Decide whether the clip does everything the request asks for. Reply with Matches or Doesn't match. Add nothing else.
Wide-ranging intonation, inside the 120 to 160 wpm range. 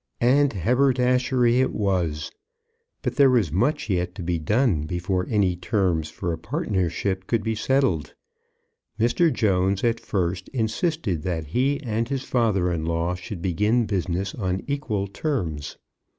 Matches